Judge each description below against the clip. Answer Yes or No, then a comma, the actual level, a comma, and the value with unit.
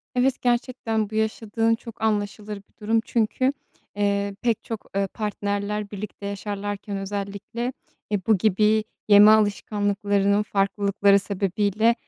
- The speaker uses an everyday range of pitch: No, narrow, 1.6 semitones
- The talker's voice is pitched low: No, high, 205 Hz